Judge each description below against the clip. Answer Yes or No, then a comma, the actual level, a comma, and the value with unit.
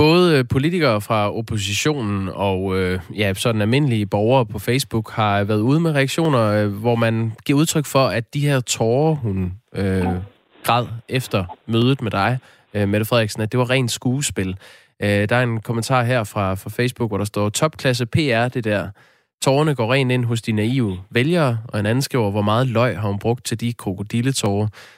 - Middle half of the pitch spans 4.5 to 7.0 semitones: No, average, 3.8 semitones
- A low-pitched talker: Yes, low, 115 Hz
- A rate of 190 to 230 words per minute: No, average, 180 wpm